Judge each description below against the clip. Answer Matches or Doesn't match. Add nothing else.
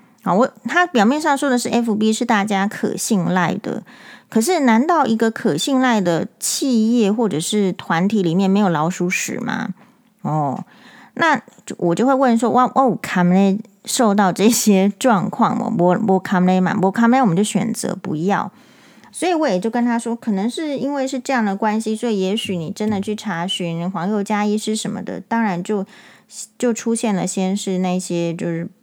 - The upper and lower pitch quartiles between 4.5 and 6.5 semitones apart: Doesn't match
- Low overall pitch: Doesn't match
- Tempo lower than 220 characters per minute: Doesn't match